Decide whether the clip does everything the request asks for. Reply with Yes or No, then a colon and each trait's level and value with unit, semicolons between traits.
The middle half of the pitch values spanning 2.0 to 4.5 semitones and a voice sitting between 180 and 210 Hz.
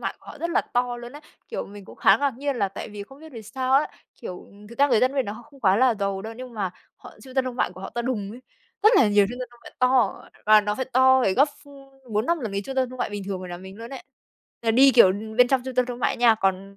No: average, 4.2 semitones; high, 240 Hz